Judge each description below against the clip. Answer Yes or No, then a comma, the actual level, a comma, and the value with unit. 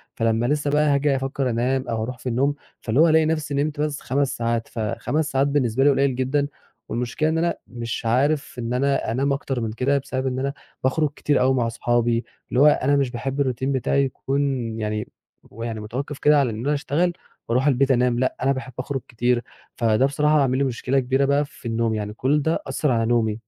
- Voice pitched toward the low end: Yes, low, 130 Hz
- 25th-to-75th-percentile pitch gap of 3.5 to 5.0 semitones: No, average, 3.0 semitones